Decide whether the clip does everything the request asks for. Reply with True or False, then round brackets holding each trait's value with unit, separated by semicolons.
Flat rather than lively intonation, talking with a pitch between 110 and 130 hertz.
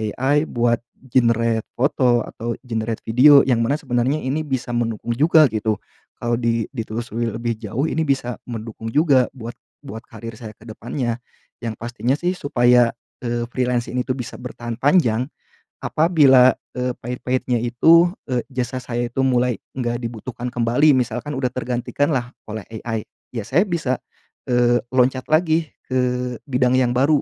True (2.2 semitones; 125 Hz)